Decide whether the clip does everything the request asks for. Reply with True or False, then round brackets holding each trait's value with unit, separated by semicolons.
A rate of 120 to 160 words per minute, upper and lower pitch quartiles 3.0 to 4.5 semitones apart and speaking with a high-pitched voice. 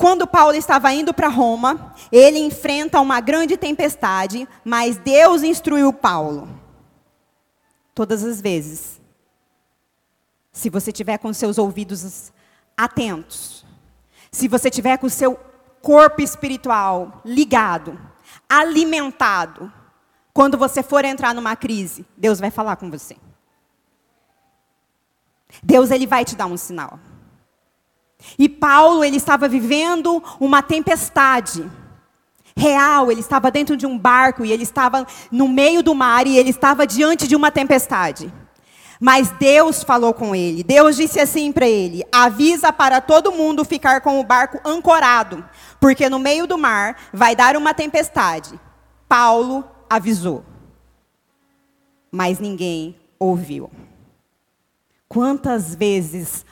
False (125 wpm; 4.9 semitones; 260 Hz)